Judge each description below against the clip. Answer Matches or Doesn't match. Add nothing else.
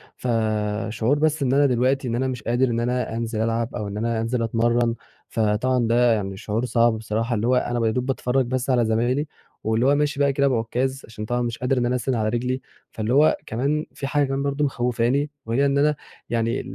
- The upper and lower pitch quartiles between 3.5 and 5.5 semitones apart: Doesn't match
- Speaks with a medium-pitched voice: Doesn't match